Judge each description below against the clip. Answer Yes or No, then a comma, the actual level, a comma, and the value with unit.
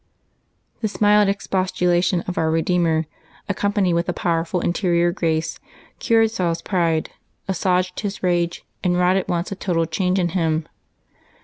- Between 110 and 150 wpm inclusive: Yes, average, 140 wpm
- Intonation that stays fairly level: Yes, narrow, 2.1 semitones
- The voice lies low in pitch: No, medium, 180 Hz